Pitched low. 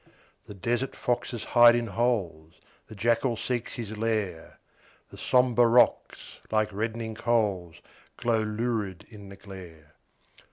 Yes: low, 110 Hz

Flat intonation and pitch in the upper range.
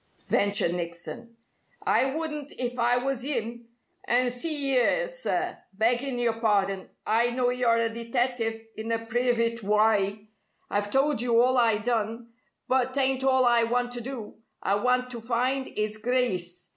Yes: narrow, 2.3 semitones; high, 235 Hz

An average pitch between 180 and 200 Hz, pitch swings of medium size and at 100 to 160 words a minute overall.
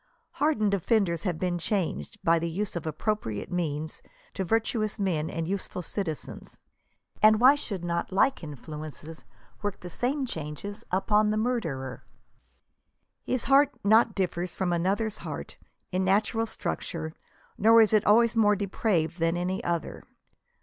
Yes: high, 190 Hz; average, 4.5 semitones; average, 150 wpm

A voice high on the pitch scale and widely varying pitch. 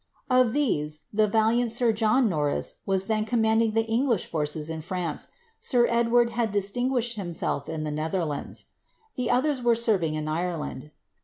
Yes: high, 215 Hz; wide, 6.5 semitones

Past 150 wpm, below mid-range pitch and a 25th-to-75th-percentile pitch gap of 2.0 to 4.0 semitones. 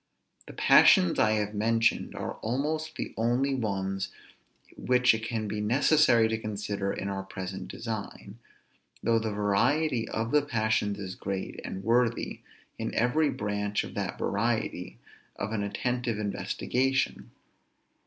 No: slow, 135 wpm; low, 110 Hz; average, 3.2 semitones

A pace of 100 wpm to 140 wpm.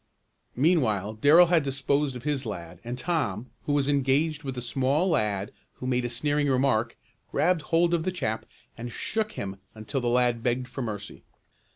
No: average, 180 wpm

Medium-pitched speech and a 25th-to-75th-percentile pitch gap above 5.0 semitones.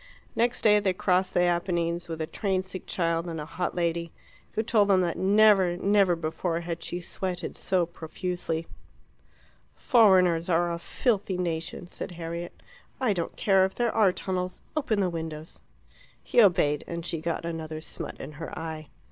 No: medium, 175 Hz; narrow, 2.4 semitones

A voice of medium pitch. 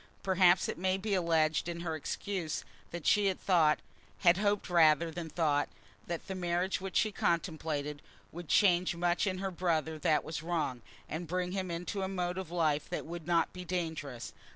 Yes: medium, 175 Hz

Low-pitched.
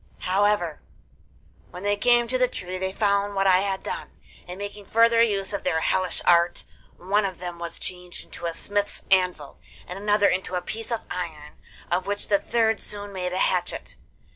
No: high, 195 Hz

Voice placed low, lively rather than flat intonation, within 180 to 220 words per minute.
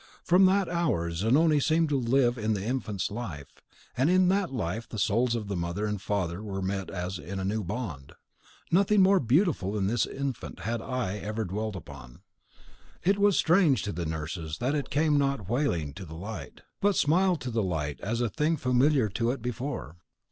Yes: low, 115 Hz; wide, 7.3 semitones; average, 190 wpm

